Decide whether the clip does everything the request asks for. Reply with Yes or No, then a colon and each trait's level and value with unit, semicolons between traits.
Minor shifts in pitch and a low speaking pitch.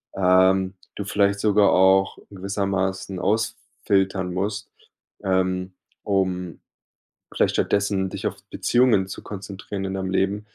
Yes: narrow, 1.3 semitones; very low, 95 Hz